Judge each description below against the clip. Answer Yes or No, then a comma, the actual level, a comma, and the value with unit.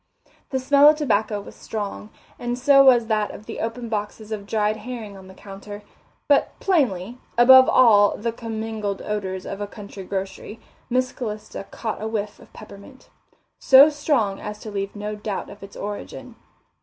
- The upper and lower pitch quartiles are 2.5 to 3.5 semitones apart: Yes, average, 3.2 semitones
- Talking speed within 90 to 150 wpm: No, average, 170 wpm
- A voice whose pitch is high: Yes, high, 215 Hz